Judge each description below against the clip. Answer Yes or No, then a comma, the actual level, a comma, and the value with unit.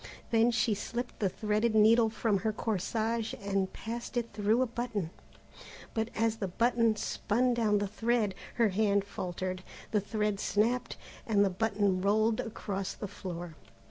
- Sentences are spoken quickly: No, average, 155 wpm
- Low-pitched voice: No, high, 215 Hz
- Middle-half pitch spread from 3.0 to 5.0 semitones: No, narrow, 2.4 semitones